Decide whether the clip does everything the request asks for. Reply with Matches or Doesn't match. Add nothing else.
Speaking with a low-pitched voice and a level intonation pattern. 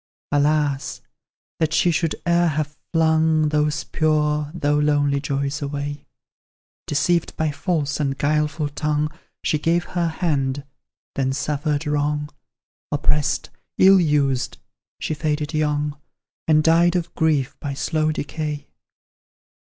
Doesn't match